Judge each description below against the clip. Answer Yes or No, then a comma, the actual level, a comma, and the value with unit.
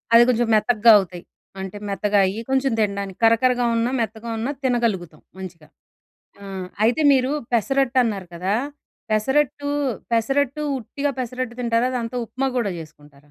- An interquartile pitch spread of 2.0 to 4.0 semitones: No, average, 4.4 semitones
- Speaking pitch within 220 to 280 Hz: Yes, high, 230 Hz